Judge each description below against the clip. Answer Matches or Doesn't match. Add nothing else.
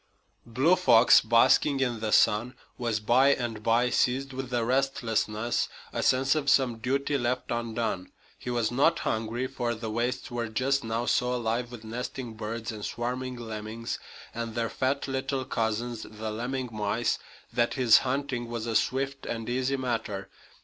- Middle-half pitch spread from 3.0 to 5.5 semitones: Doesn't match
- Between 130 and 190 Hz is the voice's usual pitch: Doesn't match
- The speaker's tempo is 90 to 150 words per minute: Doesn't match